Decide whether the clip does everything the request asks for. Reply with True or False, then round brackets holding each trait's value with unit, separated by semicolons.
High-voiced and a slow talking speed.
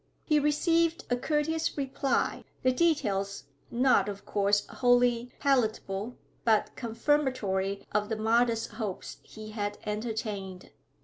True (230 Hz; 115 wpm)